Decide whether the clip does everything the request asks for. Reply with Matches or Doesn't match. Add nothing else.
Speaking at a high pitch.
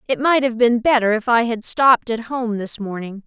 Matches